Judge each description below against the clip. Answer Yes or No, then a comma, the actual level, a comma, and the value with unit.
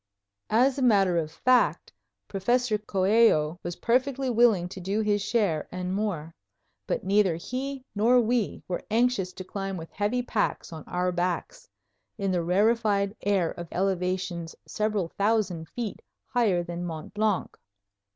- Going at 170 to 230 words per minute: No, average, 145 wpm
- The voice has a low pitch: No, high, 200 Hz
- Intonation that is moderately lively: Yes, average, 4.4 semitones